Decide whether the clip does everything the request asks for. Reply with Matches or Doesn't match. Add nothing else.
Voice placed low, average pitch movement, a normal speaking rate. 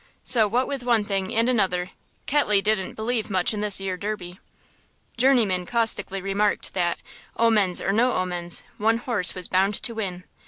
Doesn't match